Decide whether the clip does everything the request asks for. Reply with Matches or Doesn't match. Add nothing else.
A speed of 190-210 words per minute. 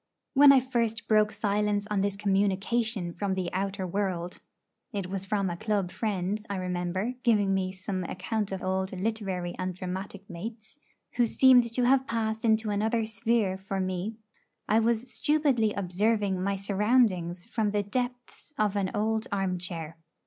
Doesn't match